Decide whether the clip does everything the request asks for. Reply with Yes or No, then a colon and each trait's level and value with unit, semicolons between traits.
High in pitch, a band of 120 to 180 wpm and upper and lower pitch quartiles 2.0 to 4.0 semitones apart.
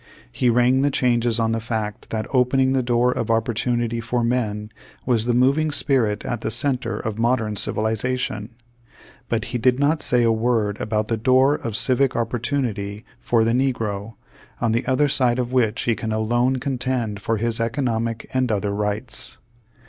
No: low, 120 Hz; average, 170 wpm; narrow, 2.4 semitones